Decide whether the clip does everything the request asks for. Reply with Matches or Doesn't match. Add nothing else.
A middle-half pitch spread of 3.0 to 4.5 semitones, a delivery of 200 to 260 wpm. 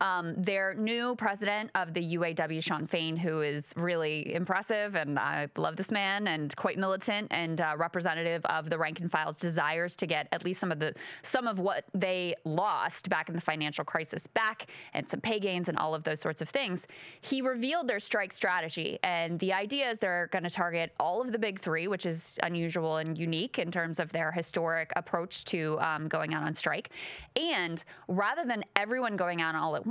Matches